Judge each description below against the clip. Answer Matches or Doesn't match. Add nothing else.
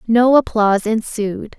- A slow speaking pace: Matches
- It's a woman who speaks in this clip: Matches